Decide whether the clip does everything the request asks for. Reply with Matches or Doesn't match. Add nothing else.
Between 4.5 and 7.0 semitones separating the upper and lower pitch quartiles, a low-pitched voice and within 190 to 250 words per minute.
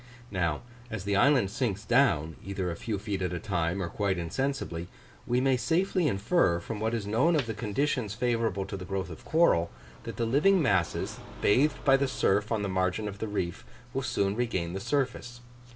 Matches